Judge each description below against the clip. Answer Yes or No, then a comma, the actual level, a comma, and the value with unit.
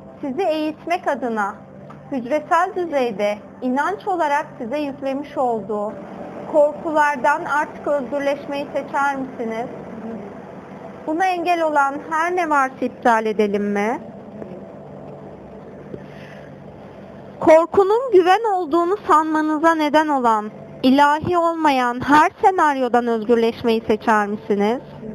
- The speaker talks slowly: Yes, slow, 90 wpm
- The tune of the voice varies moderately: No, wide, 5.7 semitones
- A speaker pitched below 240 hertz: No, very high, 280 Hz